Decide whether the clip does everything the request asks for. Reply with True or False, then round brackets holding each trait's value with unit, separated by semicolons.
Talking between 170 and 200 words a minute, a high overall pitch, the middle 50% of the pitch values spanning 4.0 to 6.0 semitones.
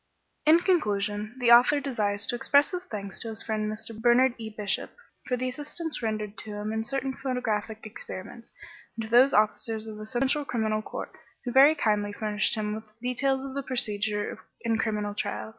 False (185 wpm; 225 Hz; 3.4 semitones)